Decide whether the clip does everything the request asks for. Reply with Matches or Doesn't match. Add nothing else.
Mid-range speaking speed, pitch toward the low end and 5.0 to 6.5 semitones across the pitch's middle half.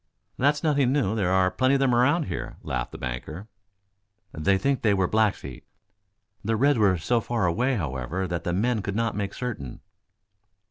Matches